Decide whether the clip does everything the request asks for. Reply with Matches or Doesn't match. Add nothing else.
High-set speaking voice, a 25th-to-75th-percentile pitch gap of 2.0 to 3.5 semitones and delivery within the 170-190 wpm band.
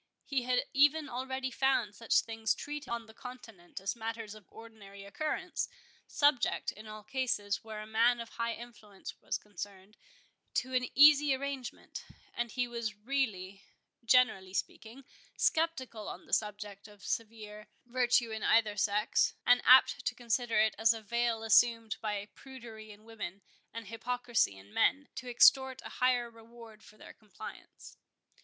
Doesn't match